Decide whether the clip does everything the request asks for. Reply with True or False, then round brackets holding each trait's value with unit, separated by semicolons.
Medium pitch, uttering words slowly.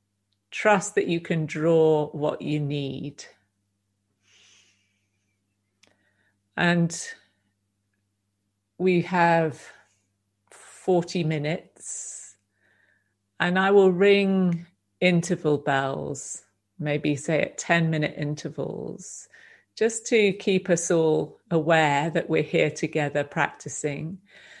True (150 Hz; 90 wpm)